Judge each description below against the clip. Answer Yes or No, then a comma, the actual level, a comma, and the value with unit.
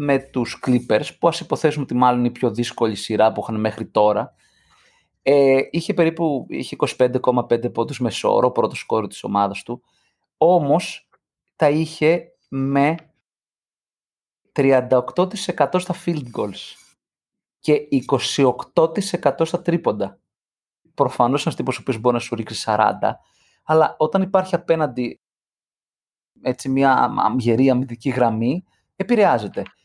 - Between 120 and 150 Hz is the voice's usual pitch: Yes, low, 135 Hz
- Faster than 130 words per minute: No, average, 125 wpm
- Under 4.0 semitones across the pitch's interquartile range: No, average, 4.9 semitones